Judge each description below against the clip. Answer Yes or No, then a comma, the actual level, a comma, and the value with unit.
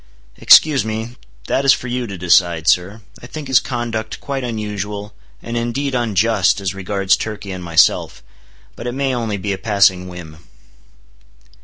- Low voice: Yes, low, 105 Hz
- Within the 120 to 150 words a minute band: No, average, 160 wpm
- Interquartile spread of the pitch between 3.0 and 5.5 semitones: Yes, average, 4.1 semitones